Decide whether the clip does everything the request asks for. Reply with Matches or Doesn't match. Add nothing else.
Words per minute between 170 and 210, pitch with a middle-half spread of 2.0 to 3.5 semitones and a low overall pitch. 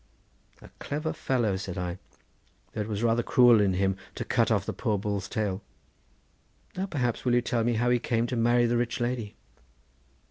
Matches